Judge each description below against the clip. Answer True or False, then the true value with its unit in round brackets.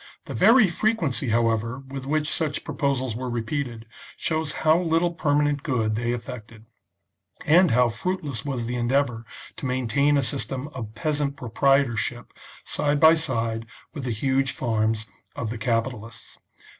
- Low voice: True (130 Hz)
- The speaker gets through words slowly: False (145 wpm)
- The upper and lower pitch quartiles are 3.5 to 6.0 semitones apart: True (4.1 semitones)